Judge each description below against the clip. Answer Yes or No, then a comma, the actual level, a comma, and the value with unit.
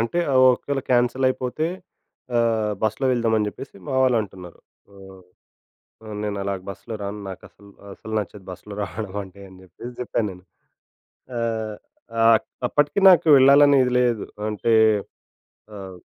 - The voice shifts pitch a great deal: No, average, 3.8 semitones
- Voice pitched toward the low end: Yes, low, 110 Hz